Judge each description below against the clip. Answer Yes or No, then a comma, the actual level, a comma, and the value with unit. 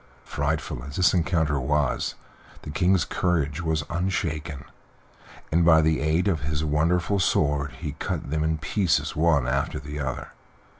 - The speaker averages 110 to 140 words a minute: No, average, 150 wpm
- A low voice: Yes, very low, 80 Hz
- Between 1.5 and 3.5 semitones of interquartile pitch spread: Yes, average, 2.7 semitones